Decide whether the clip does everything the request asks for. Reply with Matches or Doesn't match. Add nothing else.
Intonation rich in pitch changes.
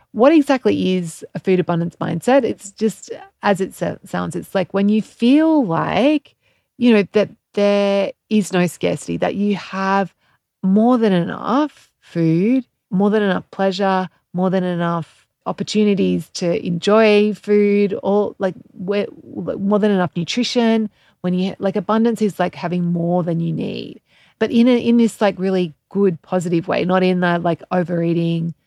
Doesn't match